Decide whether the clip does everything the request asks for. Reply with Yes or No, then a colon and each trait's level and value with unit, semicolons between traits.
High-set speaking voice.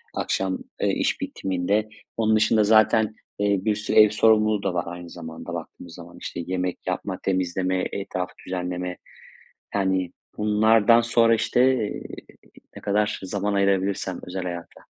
No: low, 100 Hz